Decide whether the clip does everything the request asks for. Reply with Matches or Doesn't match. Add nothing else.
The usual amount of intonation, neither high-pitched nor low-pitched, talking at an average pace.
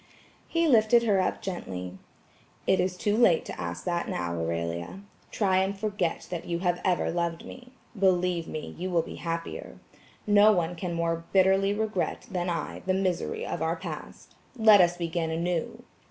Matches